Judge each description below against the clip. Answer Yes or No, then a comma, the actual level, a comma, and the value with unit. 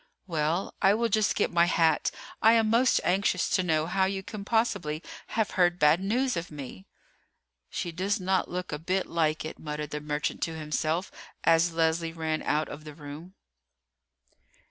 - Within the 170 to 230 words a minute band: Yes, average, 175 wpm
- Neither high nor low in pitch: Yes, medium, 170 Hz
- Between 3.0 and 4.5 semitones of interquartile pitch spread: Yes, average, 3.8 semitones